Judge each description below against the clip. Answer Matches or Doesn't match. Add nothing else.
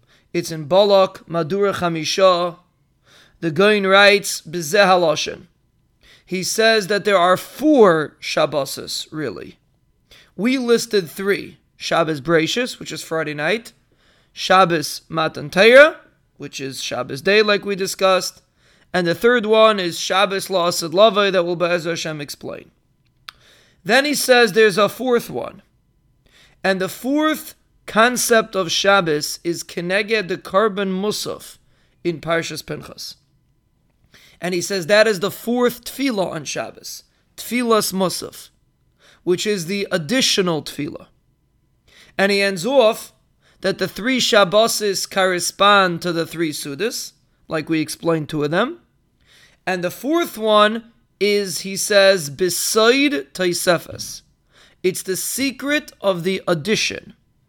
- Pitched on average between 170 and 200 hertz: Matches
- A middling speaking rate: Doesn't match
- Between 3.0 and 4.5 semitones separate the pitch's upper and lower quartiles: Matches